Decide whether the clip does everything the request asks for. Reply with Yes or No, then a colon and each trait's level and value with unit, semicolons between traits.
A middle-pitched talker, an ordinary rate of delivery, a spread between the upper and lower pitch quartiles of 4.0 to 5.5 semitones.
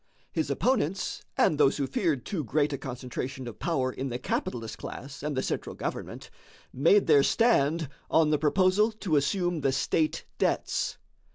Yes: medium, 150 Hz; average, 165 wpm; average, 4.6 semitones